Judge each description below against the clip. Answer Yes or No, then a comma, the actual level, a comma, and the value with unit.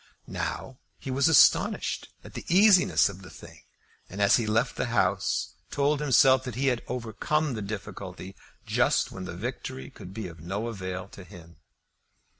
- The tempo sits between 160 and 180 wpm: Yes, average, 170 wpm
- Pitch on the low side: Yes, low, 110 Hz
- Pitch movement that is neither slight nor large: No, wide, 5.7 semitones